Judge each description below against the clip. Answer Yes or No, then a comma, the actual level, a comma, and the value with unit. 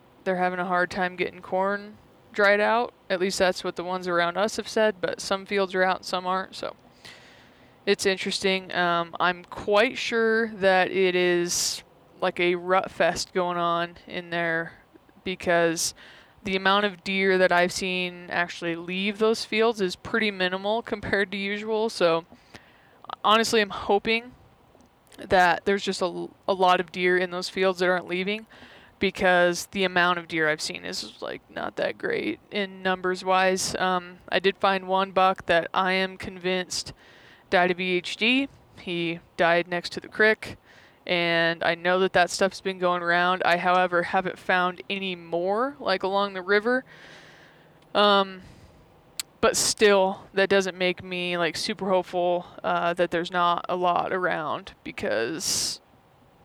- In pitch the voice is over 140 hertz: Yes, medium, 185 Hz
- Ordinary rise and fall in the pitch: No, narrow, 2.0 semitones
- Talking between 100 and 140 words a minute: No, average, 160 wpm